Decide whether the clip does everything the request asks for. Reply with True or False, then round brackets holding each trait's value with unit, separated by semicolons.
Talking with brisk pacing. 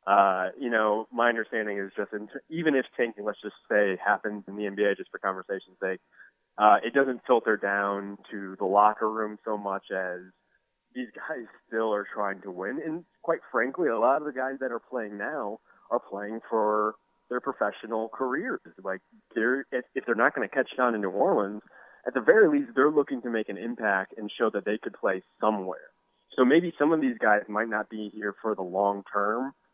True (210 wpm)